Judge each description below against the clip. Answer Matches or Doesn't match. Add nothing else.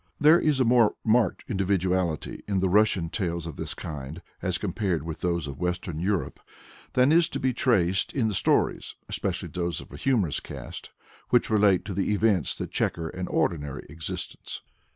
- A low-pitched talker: Matches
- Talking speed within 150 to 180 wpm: Matches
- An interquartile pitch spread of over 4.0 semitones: Matches